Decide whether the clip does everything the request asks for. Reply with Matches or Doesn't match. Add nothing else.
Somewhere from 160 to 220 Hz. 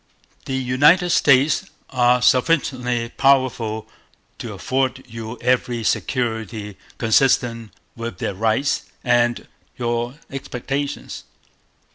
Doesn't match